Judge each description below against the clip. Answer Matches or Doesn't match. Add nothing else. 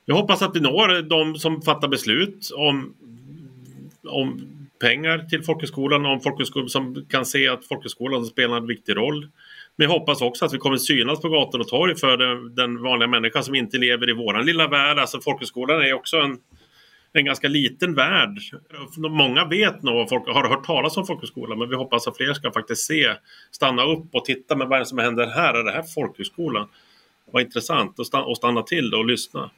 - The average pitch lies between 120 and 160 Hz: Matches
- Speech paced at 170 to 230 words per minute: Matches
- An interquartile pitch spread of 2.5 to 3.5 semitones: Doesn't match